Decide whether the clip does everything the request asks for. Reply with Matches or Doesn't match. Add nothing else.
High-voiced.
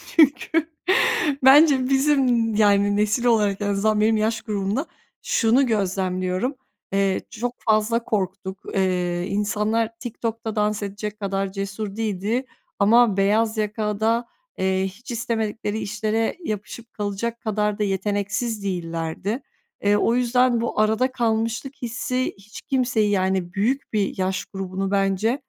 Matches